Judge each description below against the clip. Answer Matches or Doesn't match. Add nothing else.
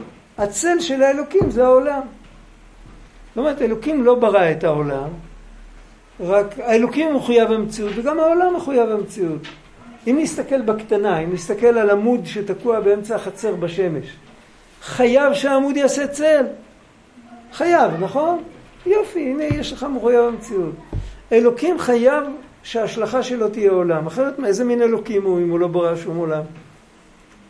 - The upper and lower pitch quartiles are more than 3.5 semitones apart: Matches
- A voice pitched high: Matches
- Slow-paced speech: Doesn't match